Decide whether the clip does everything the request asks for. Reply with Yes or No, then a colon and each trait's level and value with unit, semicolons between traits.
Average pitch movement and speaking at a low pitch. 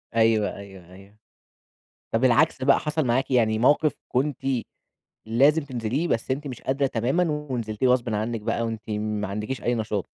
Yes: average, 3.8 semitones; low, 120 Hz